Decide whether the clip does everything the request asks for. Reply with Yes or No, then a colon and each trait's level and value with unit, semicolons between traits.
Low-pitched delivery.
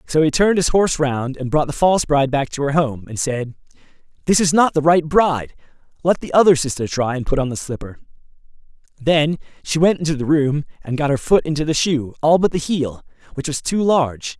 No: medium, 150 Hz